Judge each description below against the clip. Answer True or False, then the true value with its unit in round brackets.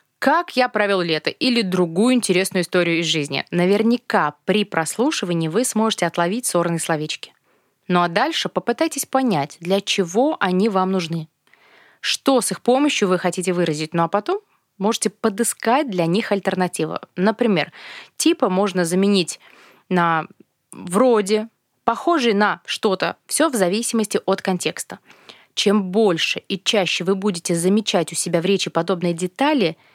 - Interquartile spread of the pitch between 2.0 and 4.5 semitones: True (4.1 semitones)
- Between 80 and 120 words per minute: False (140 wpm)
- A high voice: True (195 Hz)